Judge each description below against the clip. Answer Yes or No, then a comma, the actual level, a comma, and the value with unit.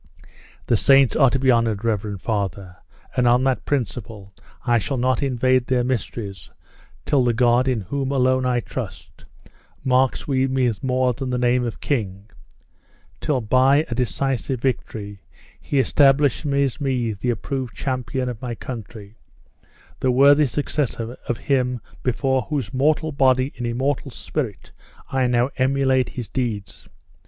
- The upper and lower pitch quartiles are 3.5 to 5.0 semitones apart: No, narrow, 2.4 semitones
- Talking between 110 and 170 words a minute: Yes, average, 145 wpm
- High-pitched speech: No, low, 125 Hz